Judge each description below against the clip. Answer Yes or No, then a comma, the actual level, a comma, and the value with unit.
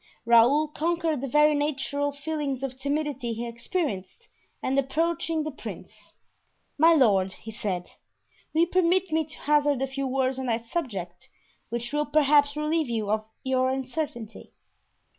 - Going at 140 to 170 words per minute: Yes, average, 150 wpm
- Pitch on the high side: Yes, very high, 275 Hz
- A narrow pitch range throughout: No, average, 4.4 semitones